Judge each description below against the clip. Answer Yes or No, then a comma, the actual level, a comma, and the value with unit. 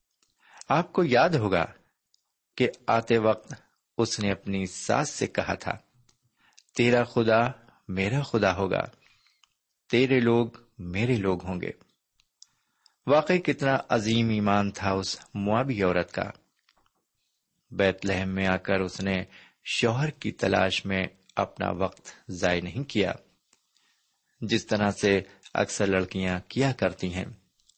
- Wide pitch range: No, average, 3.8 semitones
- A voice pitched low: Yes, low, 100 Hz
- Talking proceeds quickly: No, average, 125 wpm